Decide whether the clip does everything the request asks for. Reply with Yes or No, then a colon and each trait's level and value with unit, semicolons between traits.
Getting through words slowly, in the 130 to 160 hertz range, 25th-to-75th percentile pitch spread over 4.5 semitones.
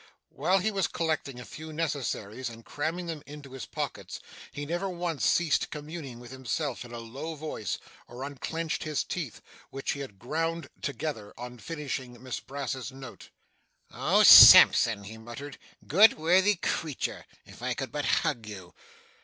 No: average, 160 wpm; medium, 140 Hz; average, 4.9 semitones